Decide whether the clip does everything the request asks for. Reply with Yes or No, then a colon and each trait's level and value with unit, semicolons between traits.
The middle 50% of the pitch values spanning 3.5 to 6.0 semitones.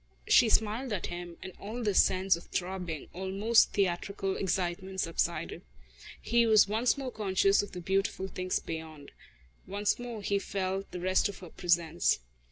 No: narrow, 2.6 semitones